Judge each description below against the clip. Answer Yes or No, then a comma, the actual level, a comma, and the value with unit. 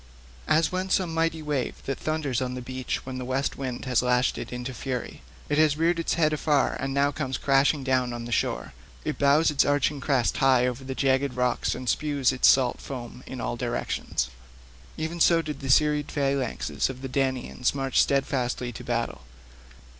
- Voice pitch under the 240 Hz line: Yes, low, 135 Hz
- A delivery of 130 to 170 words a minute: No, average, 185 wpm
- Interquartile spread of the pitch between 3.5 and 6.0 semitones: No, average, 2.8 semitones